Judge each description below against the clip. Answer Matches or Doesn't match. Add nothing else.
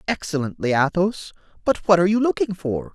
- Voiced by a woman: Doesn't match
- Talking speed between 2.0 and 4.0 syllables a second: Doesn't match